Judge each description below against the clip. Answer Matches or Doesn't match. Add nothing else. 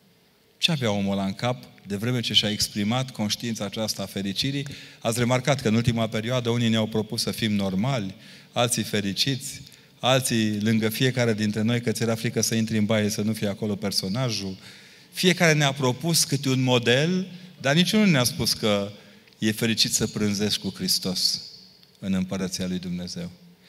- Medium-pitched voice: Doesn't match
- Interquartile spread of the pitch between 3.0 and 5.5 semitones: Matches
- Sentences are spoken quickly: Matches